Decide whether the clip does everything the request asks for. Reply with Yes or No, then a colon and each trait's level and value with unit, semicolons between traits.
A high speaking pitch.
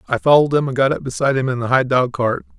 No: low, 130 Hz